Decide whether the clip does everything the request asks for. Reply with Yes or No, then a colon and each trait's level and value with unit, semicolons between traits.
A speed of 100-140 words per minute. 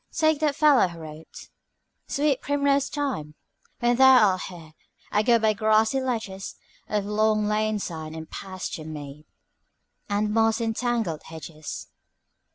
Yes: slow, 135 wpm